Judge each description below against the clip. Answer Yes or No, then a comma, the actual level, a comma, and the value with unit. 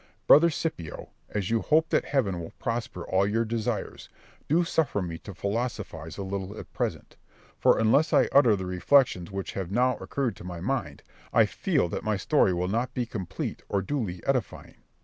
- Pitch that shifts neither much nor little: No, wide, 5.8 semitones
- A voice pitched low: Yes, low, 105 Hz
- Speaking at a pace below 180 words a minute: No, average, 185 wpm